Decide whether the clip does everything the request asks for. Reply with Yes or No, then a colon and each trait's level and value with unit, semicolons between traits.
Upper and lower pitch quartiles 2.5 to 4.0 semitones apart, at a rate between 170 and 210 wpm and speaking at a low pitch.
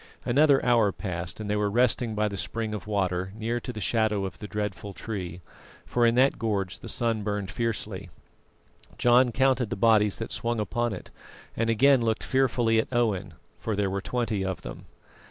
Yes: average, 3.0 semitones; average, 190 wpm; low, 110 Hz